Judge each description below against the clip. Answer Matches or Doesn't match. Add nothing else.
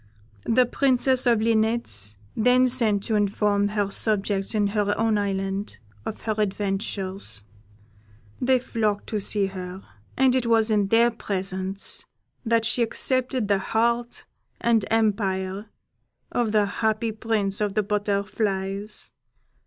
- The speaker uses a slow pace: Matches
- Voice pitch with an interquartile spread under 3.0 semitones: Matches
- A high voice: Matches